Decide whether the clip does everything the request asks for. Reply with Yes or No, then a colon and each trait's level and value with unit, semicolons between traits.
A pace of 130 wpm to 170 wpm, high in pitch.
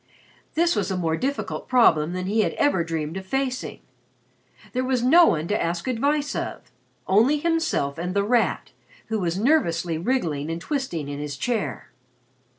Yes: average, 165 wpm; high, 200 Hz